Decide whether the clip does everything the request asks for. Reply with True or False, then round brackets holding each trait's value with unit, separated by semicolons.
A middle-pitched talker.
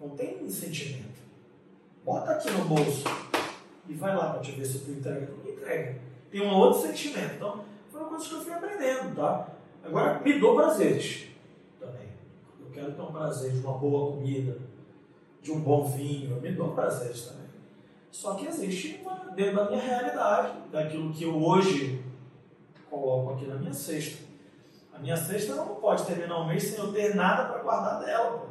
True (160 Hz)